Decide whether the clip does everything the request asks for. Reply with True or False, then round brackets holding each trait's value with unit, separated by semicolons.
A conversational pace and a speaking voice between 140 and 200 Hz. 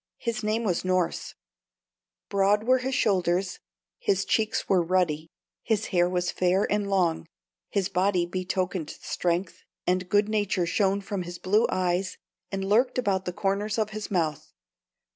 True (150 wpm; 190 Hz)